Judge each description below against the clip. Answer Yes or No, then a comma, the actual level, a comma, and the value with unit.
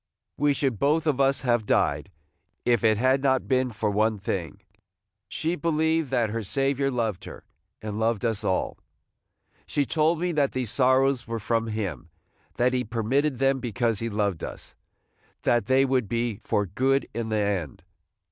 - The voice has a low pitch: Yes, low, 120 Hz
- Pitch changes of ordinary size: Yes, average, 4.0 semitones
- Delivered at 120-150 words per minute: No, average, 175 wpm